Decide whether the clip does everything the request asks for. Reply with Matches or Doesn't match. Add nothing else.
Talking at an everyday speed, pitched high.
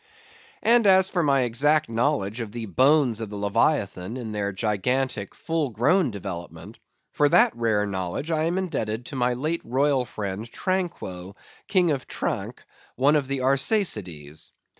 Doesn't match